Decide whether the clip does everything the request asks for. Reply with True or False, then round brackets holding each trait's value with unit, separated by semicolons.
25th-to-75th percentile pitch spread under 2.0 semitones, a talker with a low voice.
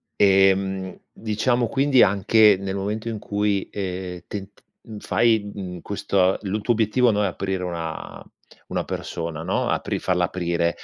False (2.6 semitones; 100 Hz)